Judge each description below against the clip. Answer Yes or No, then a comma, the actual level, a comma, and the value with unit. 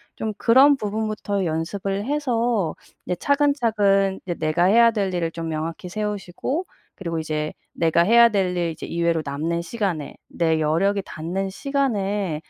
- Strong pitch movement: No, average, 4.8 semitones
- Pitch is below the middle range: No, high, 195 Hz